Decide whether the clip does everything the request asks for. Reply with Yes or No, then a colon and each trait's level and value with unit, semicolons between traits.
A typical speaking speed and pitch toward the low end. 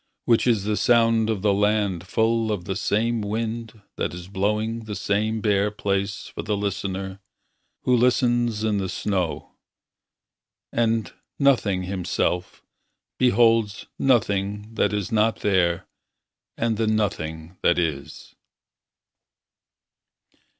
No: slow, 120 wpm; low, 105 Hz